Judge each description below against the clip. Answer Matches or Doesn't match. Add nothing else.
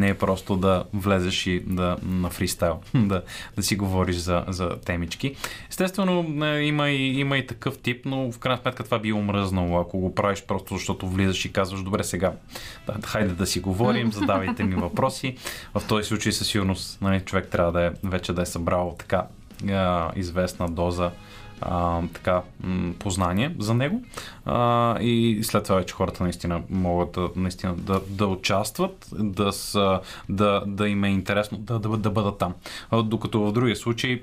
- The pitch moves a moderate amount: Matches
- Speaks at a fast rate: Matches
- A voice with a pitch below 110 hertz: Matches